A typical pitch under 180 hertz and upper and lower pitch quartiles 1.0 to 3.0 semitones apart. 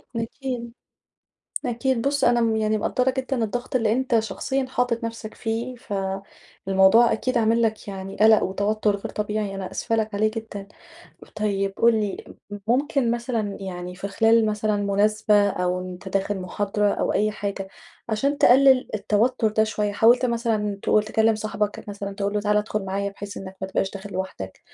No: high, 215 Hz; narrow, 2.5 semitones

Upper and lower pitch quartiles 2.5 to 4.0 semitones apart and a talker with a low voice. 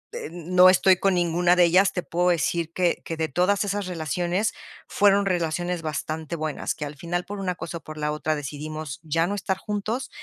No: average, 2.9 semitones; medium, 175 Hz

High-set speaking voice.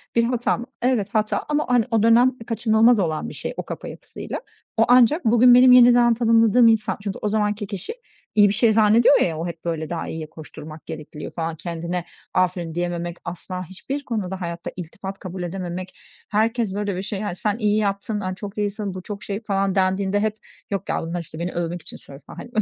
Yes: high, 200 Hz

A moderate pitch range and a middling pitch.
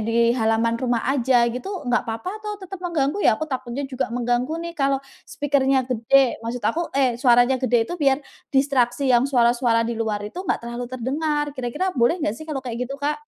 No: average, 3.0 semitones; very high, 255 Hz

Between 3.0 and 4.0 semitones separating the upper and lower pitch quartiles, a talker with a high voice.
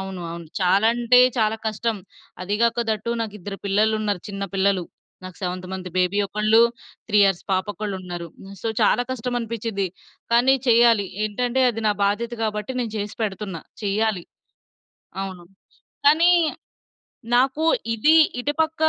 Yes: average, 3.3 semitones; high, 210 Hz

